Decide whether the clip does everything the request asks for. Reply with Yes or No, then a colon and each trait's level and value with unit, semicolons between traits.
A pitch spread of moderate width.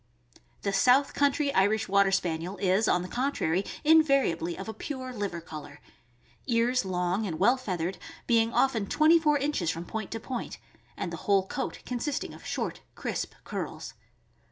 No: wide, 6.3 semitones